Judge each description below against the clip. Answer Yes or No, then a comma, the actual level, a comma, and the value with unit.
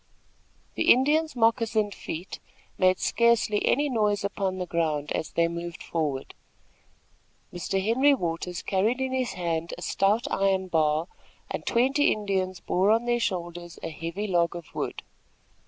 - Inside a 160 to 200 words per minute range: No, average, 145 wpm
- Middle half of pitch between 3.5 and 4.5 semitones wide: No, average, 5.2 semitones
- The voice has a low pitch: No, high, 190 Hz